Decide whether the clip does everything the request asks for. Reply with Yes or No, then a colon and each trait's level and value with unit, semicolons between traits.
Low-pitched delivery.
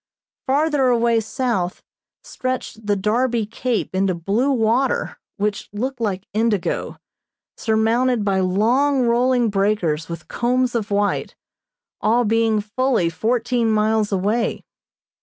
No: high, 225 Hz